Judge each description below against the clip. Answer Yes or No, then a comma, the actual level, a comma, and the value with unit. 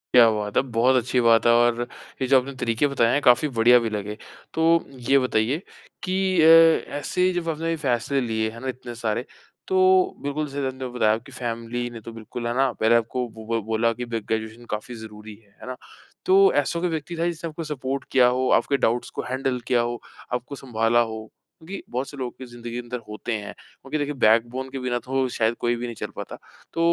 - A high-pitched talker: No, low, 120 Hz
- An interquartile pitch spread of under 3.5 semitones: Yes, average, 2.9 semitones